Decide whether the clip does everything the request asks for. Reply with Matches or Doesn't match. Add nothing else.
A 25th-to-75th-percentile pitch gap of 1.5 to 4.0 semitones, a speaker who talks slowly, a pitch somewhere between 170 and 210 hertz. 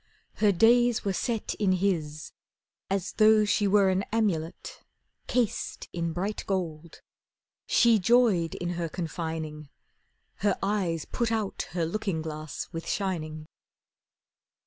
Doesn't match